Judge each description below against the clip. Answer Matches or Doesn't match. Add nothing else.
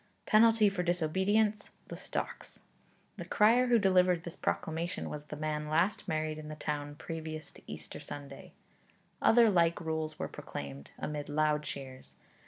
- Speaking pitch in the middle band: Matches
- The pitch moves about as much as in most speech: Matches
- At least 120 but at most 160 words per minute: Matches